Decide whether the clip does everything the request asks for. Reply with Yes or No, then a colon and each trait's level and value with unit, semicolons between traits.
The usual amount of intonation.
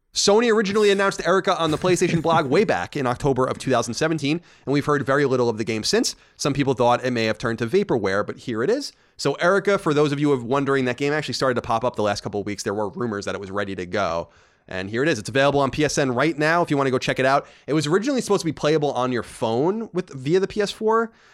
No: wide, 5.7 semitones